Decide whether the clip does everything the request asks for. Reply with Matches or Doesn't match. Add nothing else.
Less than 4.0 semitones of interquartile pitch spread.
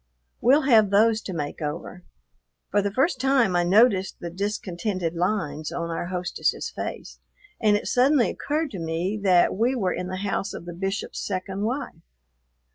Doesn't match